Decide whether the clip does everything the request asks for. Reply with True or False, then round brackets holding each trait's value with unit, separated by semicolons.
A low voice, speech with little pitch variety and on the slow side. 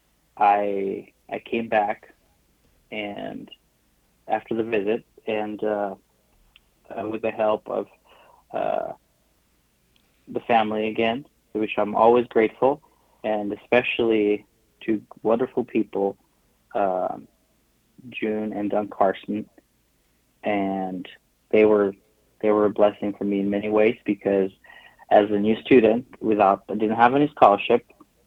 True (105 Hz; 1.6 semitones; 120 wpm)